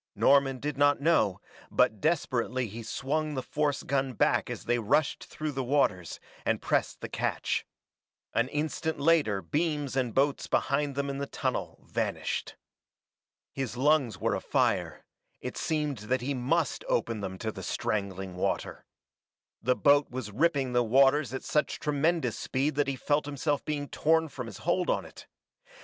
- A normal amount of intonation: Yes, average, 3.9 semitones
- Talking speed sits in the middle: Yes, average, 165 wpm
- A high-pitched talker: No, low, 135 Hz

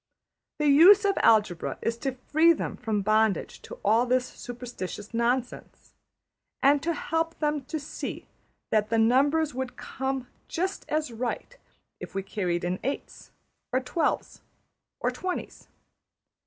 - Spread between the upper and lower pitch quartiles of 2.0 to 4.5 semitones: No, wide, 5.5 semitones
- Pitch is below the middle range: No, very high, 255 Hz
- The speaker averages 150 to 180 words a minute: No, slow, 135 wpm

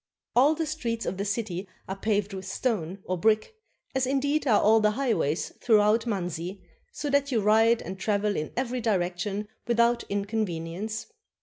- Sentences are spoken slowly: No, average, 165 wpm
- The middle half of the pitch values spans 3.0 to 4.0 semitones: Yes, average, 3.5 semitones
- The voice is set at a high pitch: Yes, high, 215 Hz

